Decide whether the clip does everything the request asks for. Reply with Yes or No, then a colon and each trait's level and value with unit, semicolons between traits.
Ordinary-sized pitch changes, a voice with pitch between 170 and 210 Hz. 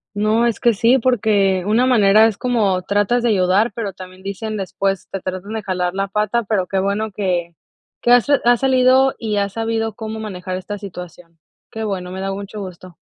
Yes: average, 3.0 semitones; high, 205 Hz